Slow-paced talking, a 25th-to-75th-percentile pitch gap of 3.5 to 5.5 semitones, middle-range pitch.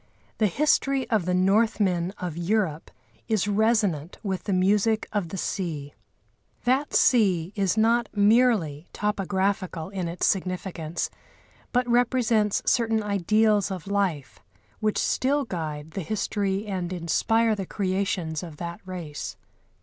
No: slow, 125 wpm; average, 3.8 semitones; high, 195 Hz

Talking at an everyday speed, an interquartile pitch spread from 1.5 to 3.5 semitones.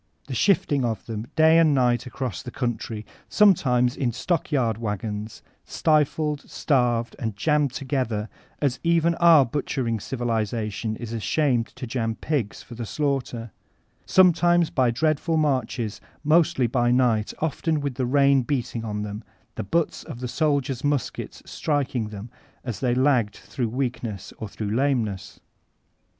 No: average, 145 wpm; average, 4.3 semitones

